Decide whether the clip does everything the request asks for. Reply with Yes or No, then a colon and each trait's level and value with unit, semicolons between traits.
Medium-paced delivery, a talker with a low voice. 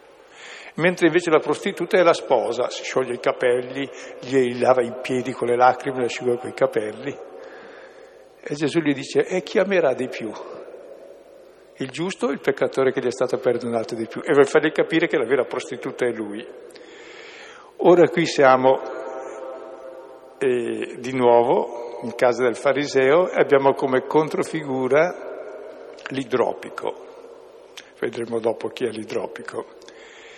No: average, 145 wpm; medium, 165 Hz